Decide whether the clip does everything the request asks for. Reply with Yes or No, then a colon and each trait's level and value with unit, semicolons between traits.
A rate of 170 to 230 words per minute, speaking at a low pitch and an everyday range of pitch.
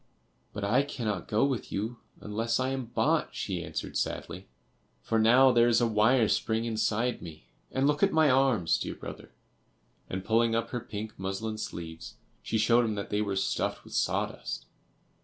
Yes: average, 175 wpm; low, 115 Hz; average, 3.0 semitones